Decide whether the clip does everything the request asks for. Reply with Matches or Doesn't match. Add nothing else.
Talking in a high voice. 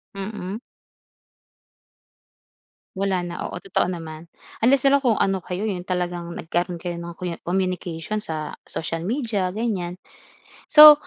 Doesn't match